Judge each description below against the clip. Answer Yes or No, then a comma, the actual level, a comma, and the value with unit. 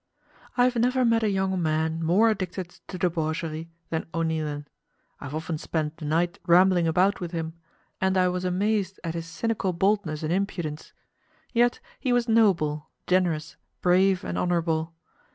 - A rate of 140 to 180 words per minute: Yes, average, 160 wpm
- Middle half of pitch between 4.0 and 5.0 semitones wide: No, average, 3.2 semitones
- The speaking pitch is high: No, medium, 175 Hz